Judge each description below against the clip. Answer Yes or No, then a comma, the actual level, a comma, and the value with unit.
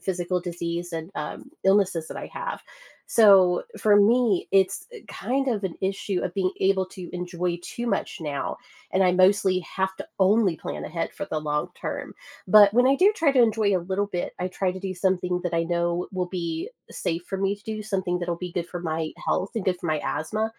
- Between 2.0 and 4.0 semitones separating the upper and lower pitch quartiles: Yes, narrow, 2.6 semitones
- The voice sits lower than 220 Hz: Yes, medium, 185 Hz